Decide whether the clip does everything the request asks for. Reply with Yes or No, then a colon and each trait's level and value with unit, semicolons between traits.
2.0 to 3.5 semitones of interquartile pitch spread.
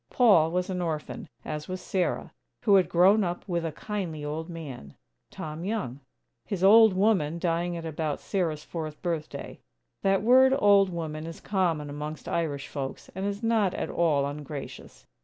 No: average, 4.2 semitones